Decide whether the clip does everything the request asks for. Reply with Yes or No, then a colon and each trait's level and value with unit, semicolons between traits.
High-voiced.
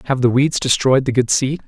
No: low, 130 Hz